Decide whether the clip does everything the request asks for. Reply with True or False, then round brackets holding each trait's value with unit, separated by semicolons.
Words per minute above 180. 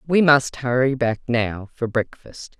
False (160 wpm)